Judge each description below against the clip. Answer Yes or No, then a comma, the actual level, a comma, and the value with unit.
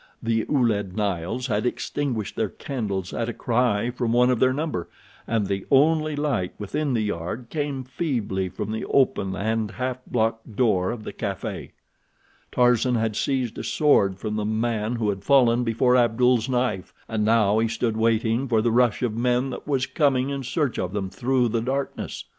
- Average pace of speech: Yes, average, 180 wpm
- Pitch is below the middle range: Yes, low, 115 Hz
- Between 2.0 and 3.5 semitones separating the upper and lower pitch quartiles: Yes, average, 3.1 semitones